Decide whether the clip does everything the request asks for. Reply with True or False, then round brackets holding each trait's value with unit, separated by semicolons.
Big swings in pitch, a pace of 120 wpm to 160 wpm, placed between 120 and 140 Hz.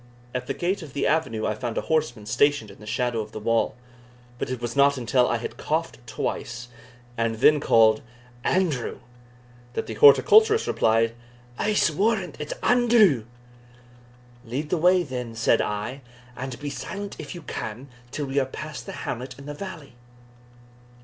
False (6.5 semitones; 170 wpm; 135 Hz)